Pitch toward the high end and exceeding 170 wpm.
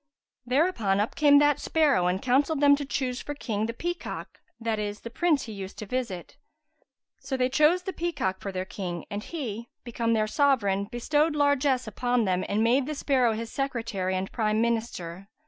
Yes: high, 240 Hz; average, 185 wpm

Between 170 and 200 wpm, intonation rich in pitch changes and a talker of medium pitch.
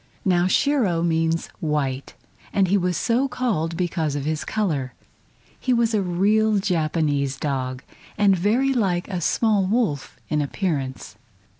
No: average, 140 wpm; wide, 5.7 semitones; medium, 175 Hz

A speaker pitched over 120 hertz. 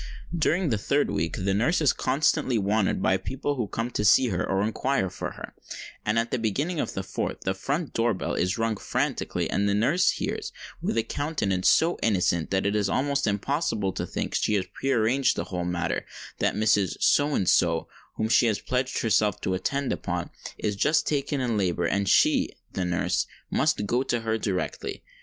No: low, 110 Hz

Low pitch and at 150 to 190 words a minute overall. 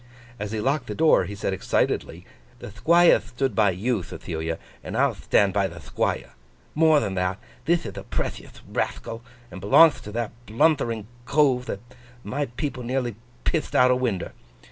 Yes: low, 115 Hz; average, 170 wpm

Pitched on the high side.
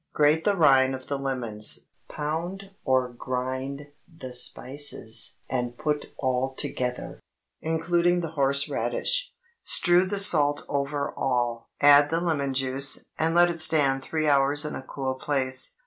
No: medium, 140 Hz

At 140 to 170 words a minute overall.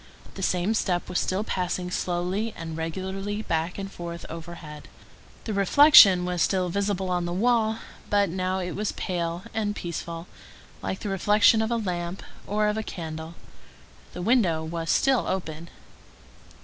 Yes: average, 155 wpm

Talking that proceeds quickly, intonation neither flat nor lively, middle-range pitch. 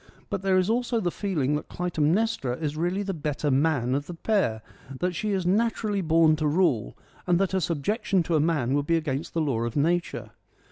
Yes: fast, 225 wpm; average, 4.7 semitones; medium, 165 Hz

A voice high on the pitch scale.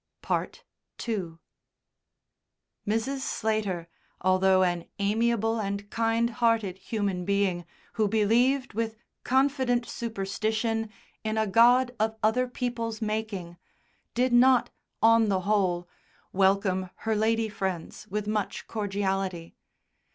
Yes: high, 215 Hz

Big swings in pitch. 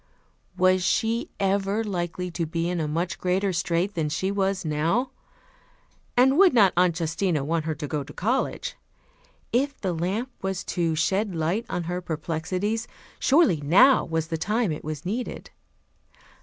No: average, 4.1 semitones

